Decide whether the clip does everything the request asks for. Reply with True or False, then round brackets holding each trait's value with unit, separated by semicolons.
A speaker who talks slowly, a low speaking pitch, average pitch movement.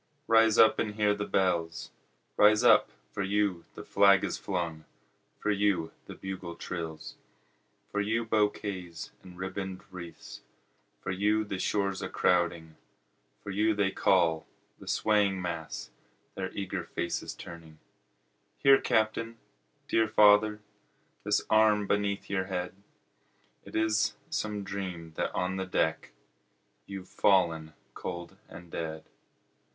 True (130 wpm; 95 Hz; 3.2 semitones)